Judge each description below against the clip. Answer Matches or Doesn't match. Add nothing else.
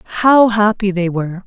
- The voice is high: Matches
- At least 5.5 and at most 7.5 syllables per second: Matches